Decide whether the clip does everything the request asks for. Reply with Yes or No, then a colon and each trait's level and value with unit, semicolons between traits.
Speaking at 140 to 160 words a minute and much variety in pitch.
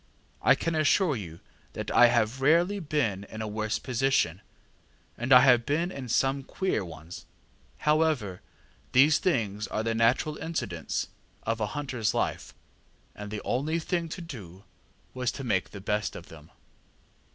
Yes: average, 155 wpm; wide, 6.3 semitones